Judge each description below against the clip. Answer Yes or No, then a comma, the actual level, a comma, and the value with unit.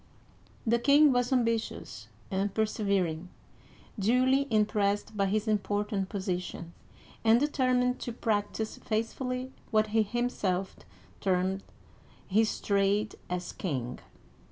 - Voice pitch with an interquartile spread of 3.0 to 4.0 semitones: Yes, average, 3.5 semitones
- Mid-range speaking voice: No, high, 215 Hz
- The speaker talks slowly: Yes, slow, 115 wpm